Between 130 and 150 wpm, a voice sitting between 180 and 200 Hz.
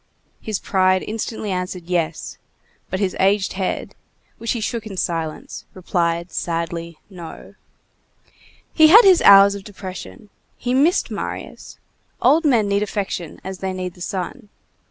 Yes: average, 140 wpm; high, 190 Hz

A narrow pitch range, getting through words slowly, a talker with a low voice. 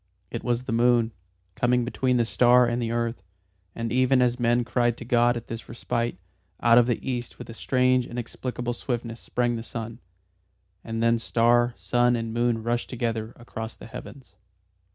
No: narrow, 1.0 semitones; average, 175 wpm; low, 120 Hz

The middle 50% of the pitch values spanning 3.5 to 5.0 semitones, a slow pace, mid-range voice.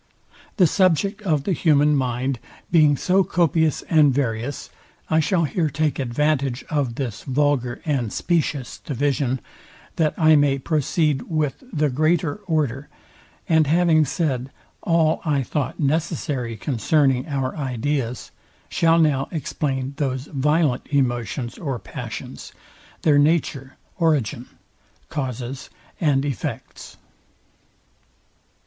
No: average, 3.1 semitones; slow, 115 wpm; medium, 145 Hz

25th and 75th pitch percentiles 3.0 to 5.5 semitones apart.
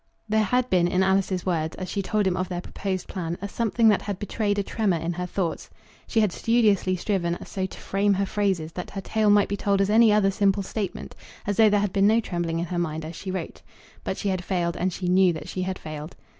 No: narrow, 2.5 semitones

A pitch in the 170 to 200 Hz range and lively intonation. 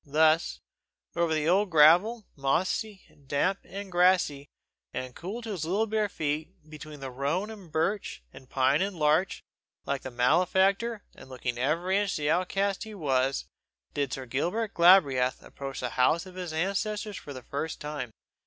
No: medium, 160 Hz; wide, 5.8 semitones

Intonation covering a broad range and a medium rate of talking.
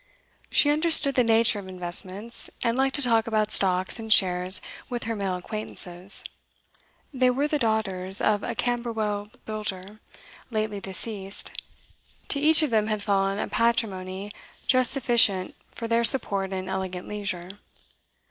No: average, 3.6 semitones; average, 145 wpm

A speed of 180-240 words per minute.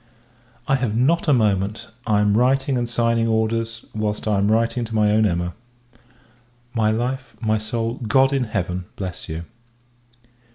No: average, 160 wpm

